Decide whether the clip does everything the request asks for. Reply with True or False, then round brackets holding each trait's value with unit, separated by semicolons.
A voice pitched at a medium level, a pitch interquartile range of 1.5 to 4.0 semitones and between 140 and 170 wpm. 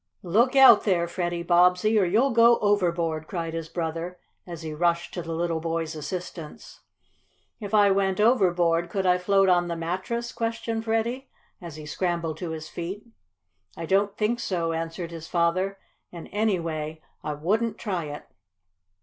True (175 Hz; 3.7 semitones; 160 wpm)